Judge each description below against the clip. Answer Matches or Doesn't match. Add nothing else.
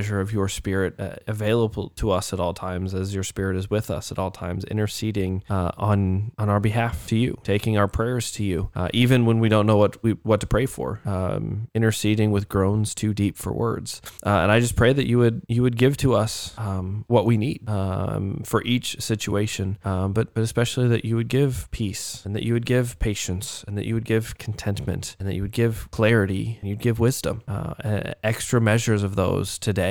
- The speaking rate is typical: Doesn't match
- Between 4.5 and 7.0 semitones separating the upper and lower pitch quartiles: Doesn't match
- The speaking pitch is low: Matches